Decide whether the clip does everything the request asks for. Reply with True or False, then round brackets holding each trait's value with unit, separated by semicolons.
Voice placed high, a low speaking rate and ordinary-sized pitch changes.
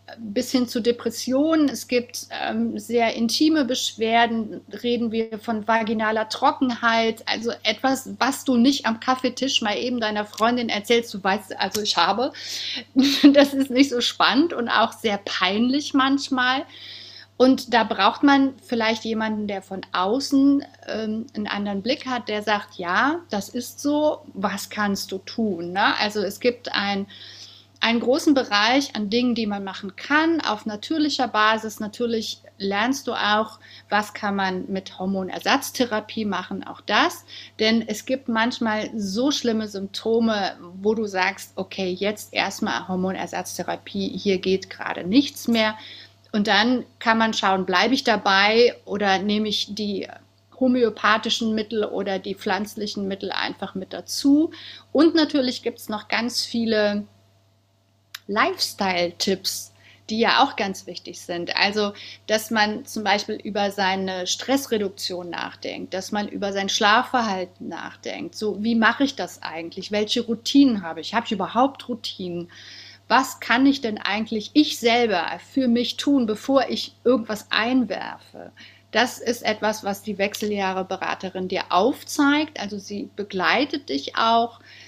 False (220 Hz; 145 wpm; 3.7 semitones)